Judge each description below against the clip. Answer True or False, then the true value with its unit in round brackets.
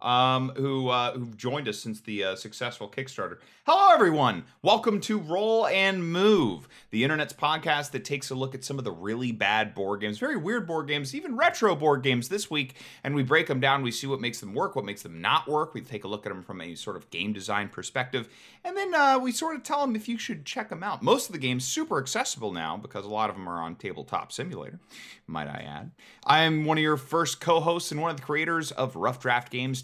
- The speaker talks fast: True (240 wpm)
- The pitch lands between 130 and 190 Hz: True (135 Hz)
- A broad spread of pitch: True (5.9 semitones)